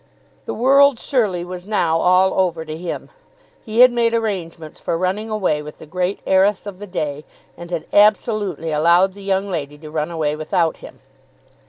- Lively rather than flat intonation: No, average, 4.2 semitones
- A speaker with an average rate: Yes, average, 180 wpm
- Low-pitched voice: No, medium, 185 Hz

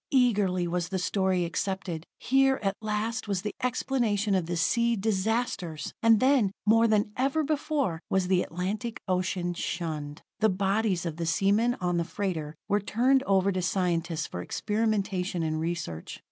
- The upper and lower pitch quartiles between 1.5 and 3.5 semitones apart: No, average, 4.1 semitones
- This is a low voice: No, high, 195 Hz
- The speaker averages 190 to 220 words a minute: No, average, 160 wpm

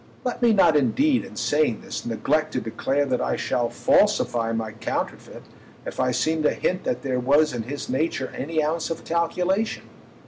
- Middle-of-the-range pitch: Yes, medium, 150 Hz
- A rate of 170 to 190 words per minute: Yes, average, 180 wpm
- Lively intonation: No, average, 5.0 semitones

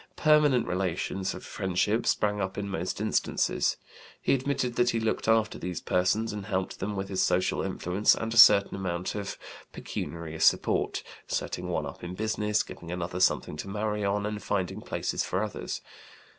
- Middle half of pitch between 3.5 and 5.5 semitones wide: No, average, 2.9 semitones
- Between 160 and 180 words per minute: Yes, average, 170 wpm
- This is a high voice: No, low, 100 Hz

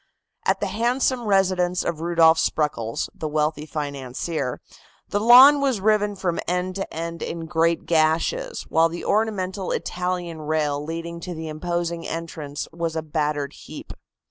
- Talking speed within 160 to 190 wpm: No, average, 145 wpm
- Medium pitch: Yes, medium, 170 Hz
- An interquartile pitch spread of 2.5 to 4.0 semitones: Yes, average, 3.2 semitones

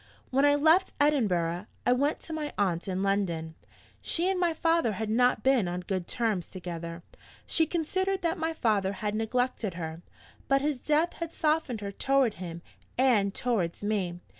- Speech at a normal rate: Yes, average, 170 wpm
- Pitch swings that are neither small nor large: No, wide, 8.2 semitones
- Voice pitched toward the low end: No, high, 225 Hz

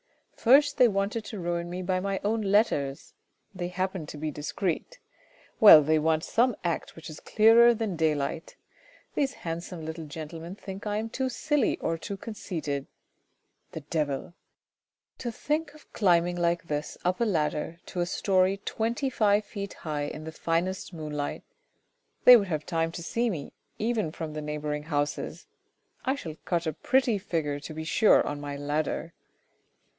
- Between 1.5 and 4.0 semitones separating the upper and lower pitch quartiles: No, average, 5.3 semitones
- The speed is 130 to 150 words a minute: No, average, 170 wpm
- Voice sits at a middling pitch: Yes, medium, 175 Hz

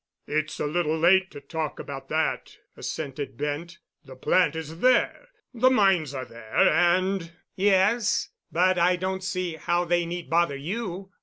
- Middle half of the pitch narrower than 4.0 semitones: Yes, average, 3.5 semitones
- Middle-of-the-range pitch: Yes, medium, 175 Hz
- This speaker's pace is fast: No, average, 155 wpm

